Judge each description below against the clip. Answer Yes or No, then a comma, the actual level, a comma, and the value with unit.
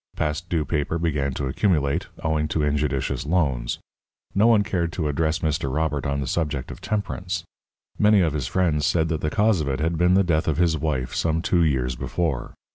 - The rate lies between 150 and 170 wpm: No, average, 200 wpm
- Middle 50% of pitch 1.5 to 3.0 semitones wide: No, average, 3.4 semitones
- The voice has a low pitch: Yes, very low, 80 Hz